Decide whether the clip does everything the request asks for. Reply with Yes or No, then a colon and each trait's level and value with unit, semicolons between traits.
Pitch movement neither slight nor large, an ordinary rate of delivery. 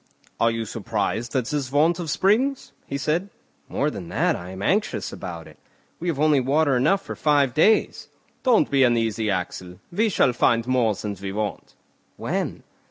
No: wide, 6.4 semitones; average, 175 wpm